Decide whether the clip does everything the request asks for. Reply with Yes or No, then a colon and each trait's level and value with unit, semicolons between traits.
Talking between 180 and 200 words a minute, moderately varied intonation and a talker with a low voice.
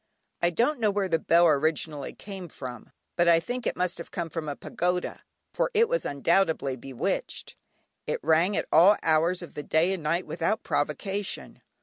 No: average, 185 wpm; average, 3.5 semitones; medium, 170 Hz